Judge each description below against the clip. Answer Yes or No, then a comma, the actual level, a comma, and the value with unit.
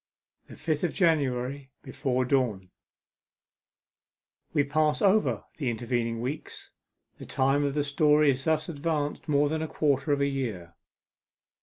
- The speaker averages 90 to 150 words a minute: Yes, average, 140 wpm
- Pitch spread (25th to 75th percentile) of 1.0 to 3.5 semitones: Yes, average, 3.1 semitones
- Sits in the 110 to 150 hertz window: Yes, medium, 140 Hz